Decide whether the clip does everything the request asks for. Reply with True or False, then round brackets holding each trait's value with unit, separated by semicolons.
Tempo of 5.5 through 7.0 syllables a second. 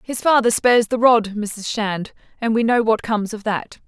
False (5.0 syllables/s)